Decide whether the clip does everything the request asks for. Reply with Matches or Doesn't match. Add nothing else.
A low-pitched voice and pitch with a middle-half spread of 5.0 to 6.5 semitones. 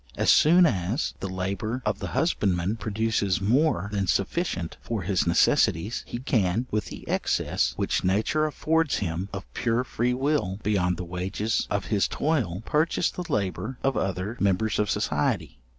Matches